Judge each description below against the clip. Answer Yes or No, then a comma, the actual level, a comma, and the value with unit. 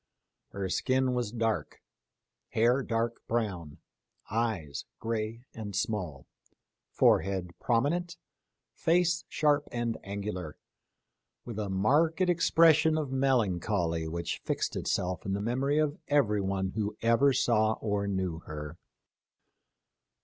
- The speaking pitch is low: Yes, low, 110 Hz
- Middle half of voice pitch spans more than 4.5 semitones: Yes, wide, 5.6 semitones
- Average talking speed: No, slow, 110 wpm